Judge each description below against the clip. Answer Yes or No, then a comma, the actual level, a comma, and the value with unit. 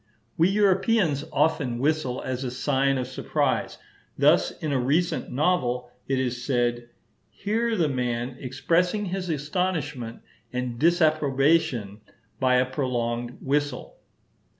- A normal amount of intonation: Yes, average, 4.8 semitones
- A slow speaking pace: Yes, slow, 120 wpm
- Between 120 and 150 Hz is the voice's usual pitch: Yes, low, 135 Hz